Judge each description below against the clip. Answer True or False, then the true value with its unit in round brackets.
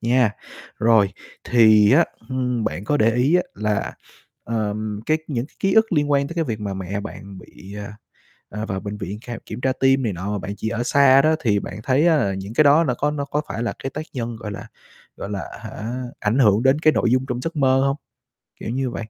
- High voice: False (120 Hz)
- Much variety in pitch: False (4.8 semitones)